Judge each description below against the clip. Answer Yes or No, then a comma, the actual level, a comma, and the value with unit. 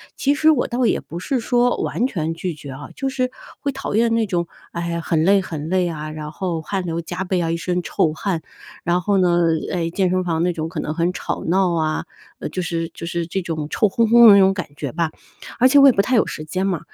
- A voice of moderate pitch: Yes, medium, 180 Hz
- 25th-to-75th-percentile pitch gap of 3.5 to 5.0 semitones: Yes, average, 3.8 semitones